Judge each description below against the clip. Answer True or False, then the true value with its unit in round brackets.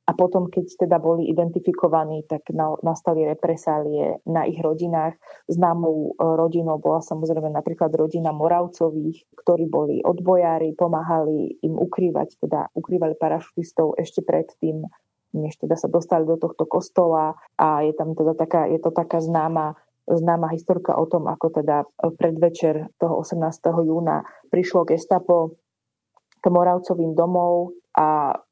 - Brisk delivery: False (135 wpm)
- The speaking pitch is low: False (165 Hz)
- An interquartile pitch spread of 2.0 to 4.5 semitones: False (1.6 semitones)